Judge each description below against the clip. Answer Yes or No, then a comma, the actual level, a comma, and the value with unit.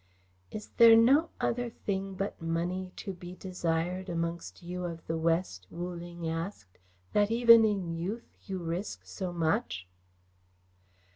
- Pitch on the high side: No, medium, 180 Hz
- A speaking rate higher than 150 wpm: No, average, 140 wpm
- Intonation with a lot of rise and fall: No, average, 3.3 semitones